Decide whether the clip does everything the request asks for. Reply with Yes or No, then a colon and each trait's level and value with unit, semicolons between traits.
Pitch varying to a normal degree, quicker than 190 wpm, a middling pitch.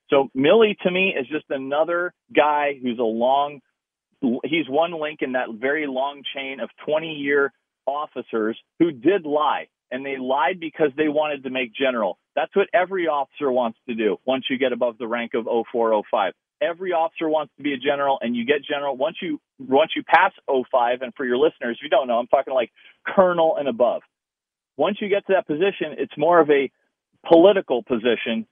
Yes: average, 4.1 semitones; average, 200 wpm; medium, 145 Hz